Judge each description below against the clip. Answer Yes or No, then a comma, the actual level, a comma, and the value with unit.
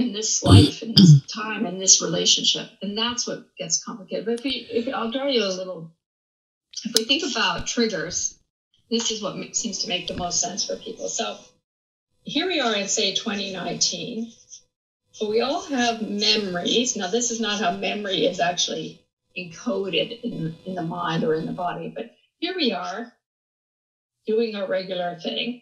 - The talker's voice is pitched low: No, high, 220 Hz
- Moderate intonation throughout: Yes, average, 4.1 semitones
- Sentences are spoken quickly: No, average, 180 wpm